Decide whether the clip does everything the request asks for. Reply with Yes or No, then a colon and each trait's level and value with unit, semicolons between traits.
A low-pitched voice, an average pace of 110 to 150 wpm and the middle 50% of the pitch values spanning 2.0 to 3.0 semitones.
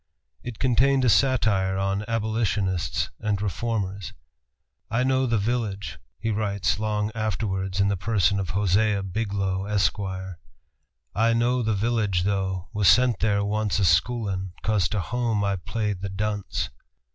Yes: low, 105 Hz; average, 145 wpm; average, 2.7 semitones